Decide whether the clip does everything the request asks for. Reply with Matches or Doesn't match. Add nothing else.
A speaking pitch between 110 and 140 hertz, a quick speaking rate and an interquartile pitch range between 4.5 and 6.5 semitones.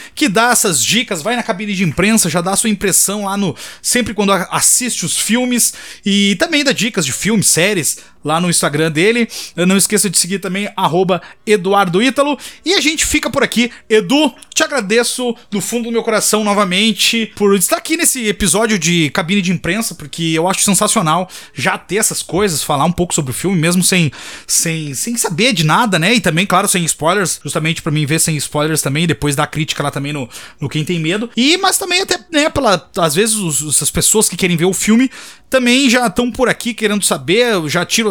Doesn't match